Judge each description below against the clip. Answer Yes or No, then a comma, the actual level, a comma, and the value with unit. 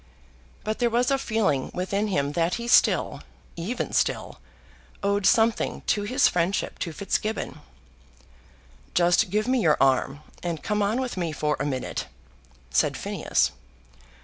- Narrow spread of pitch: No, average, 5.0 semitones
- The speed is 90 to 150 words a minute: Yes, average, 145 wpm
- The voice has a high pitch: Yes, high, 200 Hz